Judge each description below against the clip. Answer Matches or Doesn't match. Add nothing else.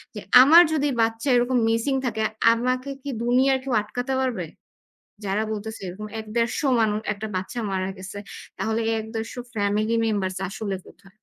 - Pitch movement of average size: Matches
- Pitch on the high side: Matches